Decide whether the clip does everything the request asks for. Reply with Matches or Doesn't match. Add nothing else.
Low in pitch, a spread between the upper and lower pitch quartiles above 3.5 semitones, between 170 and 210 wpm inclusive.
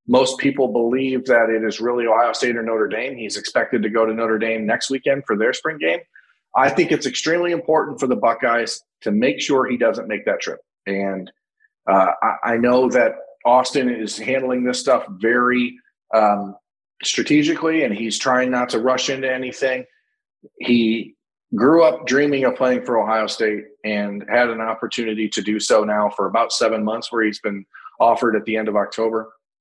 Doesn't match